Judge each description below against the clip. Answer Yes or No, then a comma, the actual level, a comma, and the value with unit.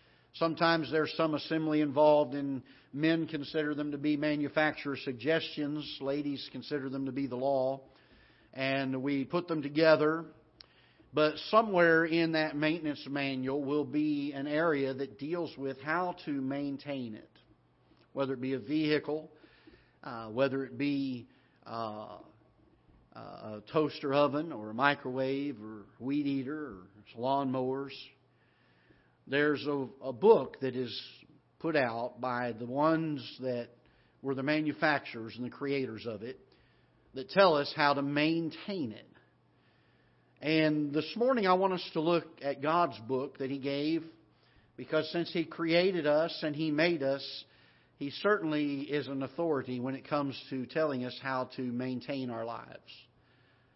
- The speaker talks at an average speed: Yes, average, 145 wpm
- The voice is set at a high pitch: No, medium, 140 Hz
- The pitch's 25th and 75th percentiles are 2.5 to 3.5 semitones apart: Yes, average, 2.8 semitones